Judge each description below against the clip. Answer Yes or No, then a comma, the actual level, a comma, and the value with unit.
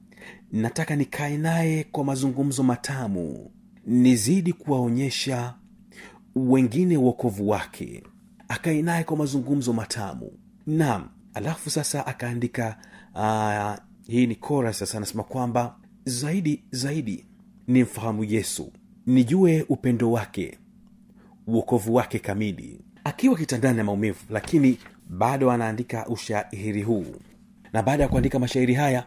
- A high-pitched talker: No, low, 130 Hz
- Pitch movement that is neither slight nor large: No, wide, 5.8 semitones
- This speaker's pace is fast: No, average, 110 wpm